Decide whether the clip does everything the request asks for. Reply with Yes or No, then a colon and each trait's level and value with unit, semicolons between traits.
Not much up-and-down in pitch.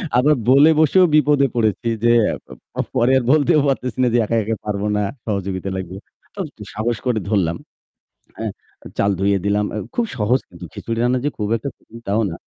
No: average, 4.6 semitones